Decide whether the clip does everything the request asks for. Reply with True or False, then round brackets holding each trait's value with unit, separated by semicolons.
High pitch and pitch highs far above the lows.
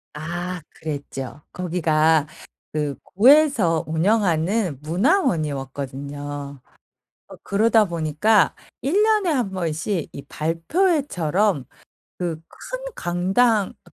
False (175 Hz; 6.1 semitones)